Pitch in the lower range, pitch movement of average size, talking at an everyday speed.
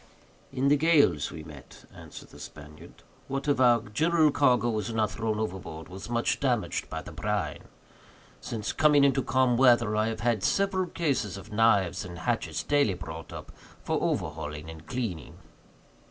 No: low, 115 Hz; wide, 6.3 semitones; average, 165 wpm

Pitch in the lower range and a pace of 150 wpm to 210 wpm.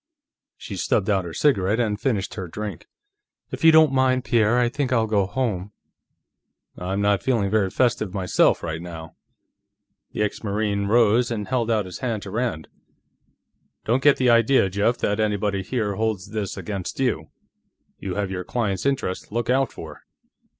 Yes: low, 105 Hz; average, 170 wpm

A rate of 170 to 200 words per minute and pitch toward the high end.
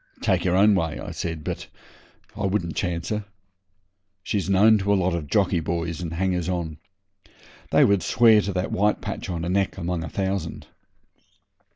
No: average, 180 wpm; very low, 90 Hz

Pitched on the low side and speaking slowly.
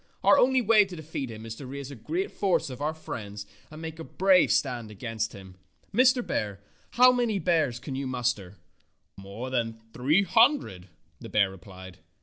No: low, 130 Hz; average, 180 wpm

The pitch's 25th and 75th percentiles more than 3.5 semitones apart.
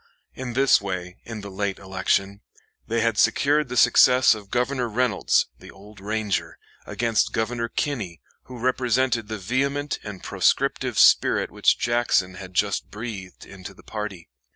Yes: average, 4.1 semitones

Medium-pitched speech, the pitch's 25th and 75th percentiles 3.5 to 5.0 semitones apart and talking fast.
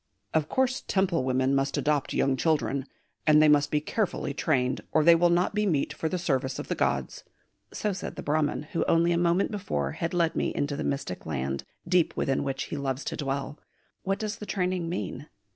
Yes: medium, 155 Hz; average, 4.3 semitones; fast, 210 wpm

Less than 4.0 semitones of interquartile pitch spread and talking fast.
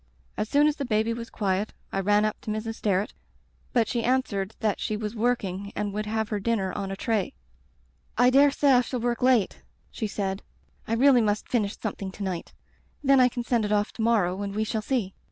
Yes: average, 3.0 semitones; fast, 220 wpm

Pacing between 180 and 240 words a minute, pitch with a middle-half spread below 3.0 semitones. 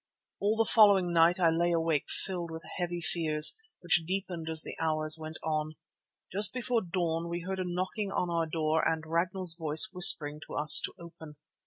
Yes: average, 185 wpm; narrow, 2.4 semitones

